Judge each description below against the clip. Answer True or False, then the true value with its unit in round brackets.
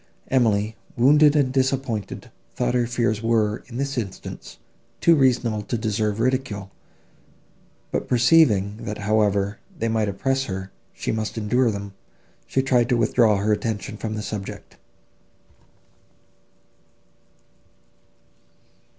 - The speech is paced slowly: True (115 wpm)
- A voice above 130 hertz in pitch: False (115 Hz)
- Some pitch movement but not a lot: True (3.5 semitones)